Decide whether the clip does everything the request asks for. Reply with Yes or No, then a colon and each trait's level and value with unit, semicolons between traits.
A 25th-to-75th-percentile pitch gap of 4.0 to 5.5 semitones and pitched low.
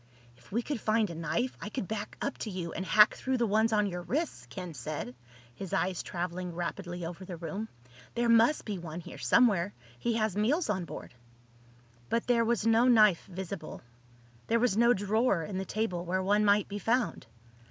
No: average, 4.4 semitones; high, 205 Hz